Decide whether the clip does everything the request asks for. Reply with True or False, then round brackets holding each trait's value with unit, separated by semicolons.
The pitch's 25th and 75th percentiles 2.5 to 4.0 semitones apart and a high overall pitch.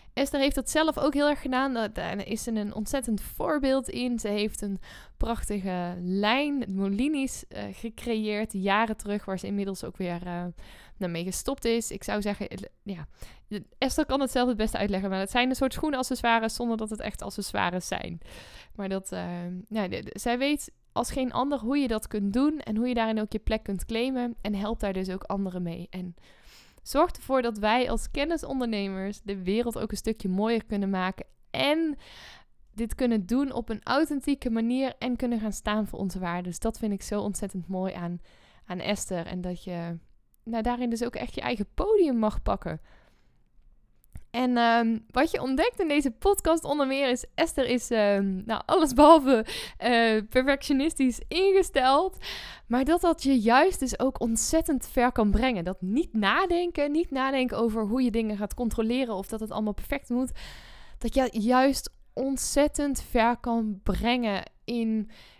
False (4.7 semitones; 230 Hz)